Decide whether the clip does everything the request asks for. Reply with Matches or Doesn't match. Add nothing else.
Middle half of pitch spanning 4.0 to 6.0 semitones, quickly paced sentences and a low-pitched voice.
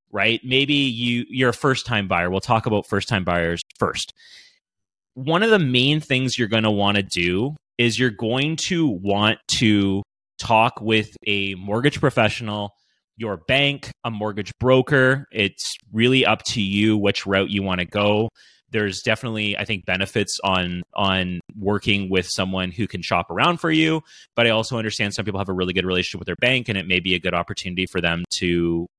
Doesn't match